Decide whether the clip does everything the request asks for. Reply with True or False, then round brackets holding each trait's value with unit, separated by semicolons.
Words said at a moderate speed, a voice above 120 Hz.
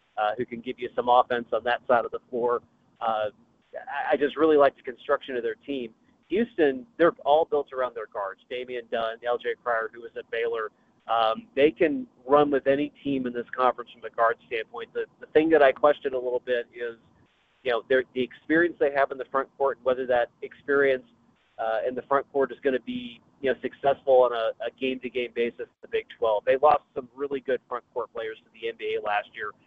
False (225 wpm; 135 Hz)